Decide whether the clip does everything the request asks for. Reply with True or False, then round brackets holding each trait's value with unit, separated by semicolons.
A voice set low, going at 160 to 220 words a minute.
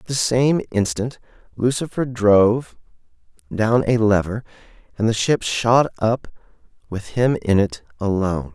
False (110 Hz; 135 wpm)